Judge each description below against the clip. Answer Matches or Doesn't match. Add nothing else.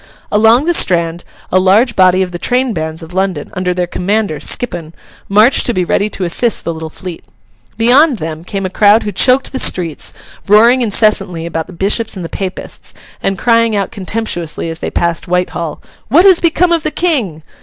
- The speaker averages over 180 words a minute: Matches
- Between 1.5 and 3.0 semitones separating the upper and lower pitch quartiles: Doesn't match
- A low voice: Doesn't match